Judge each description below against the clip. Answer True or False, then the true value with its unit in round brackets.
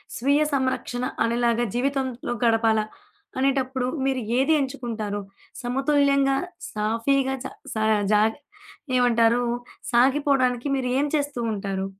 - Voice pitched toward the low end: False (250 Hz)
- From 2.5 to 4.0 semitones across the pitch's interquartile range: True (2.9 semitones)